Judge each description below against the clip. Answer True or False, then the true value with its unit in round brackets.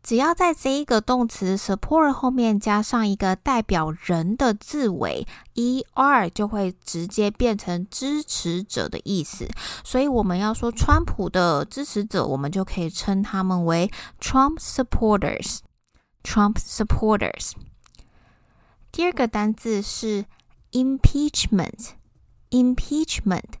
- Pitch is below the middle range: False (215 Hz)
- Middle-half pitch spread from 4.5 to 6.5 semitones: True (5.0 semitones)